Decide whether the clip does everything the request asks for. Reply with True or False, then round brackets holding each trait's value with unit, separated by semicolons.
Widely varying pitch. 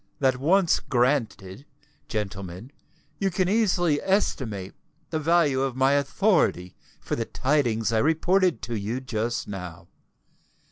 True (7.1 semitones)